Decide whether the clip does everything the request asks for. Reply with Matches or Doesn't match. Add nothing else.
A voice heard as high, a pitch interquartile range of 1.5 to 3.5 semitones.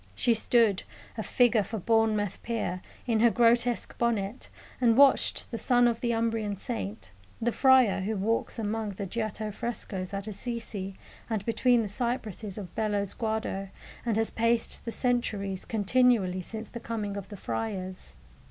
Matches